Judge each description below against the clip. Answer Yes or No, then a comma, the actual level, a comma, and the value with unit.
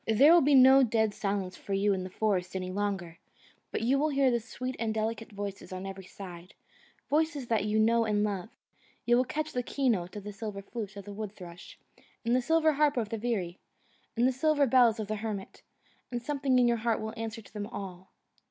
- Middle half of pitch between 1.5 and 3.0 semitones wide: No, average, 4.2 semitones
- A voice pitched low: No, high, 220 Hz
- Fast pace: Yes, fast, 215 wpm